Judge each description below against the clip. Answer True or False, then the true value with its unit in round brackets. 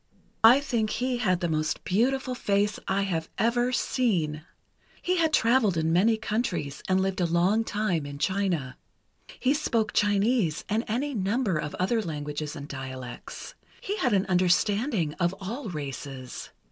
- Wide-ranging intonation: True (6.3 semitones)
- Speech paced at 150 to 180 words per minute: True (155 wpm)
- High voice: True (200 Hz)